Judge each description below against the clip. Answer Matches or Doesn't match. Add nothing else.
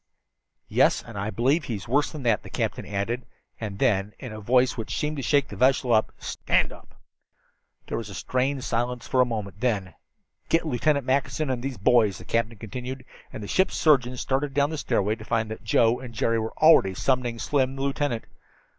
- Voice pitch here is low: Matches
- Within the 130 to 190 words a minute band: Doesn't match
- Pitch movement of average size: Matches